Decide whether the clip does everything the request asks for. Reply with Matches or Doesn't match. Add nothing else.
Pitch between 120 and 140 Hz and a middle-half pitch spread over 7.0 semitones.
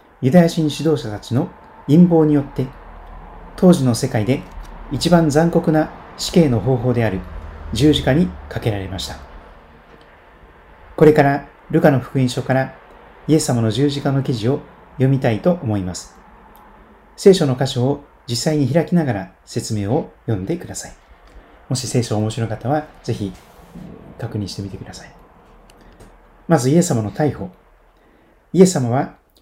Doesn't match